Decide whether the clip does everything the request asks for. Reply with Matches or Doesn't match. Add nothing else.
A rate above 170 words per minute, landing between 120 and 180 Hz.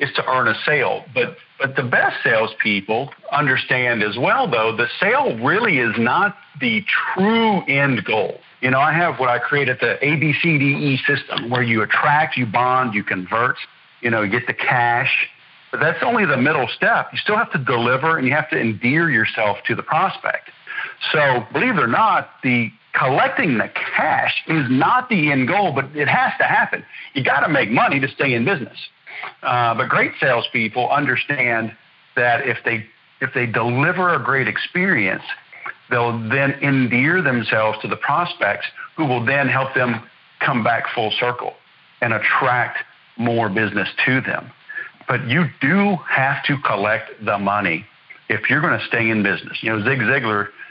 Matches